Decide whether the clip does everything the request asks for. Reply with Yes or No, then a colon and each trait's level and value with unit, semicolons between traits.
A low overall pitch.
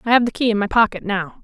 No: high, 215 Hz